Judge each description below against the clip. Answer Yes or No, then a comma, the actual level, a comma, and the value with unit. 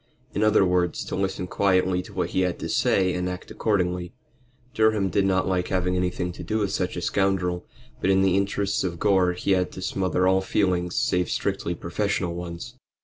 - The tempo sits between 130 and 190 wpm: No, average, 200 wpm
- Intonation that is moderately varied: No, narrow, 1.5 semitones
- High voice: No, very low, 95 Hz